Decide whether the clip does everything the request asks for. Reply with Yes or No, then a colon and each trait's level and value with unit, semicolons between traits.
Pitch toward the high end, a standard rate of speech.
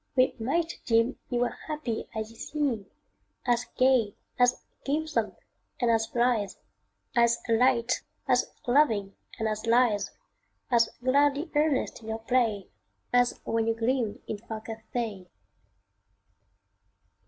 No: high, 235 Hz; slow, 125 wpm